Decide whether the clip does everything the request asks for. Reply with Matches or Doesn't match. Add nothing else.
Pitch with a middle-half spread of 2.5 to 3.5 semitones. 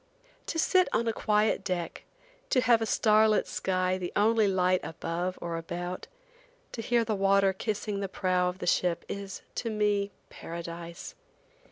Matches